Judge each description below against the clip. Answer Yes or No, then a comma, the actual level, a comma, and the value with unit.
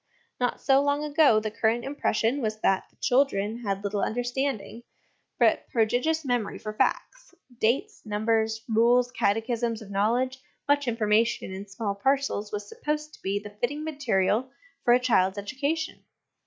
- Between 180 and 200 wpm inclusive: No, average, 150 wpm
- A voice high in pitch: Yes, high, 230 Hz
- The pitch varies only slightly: No, average, 4.4 semitones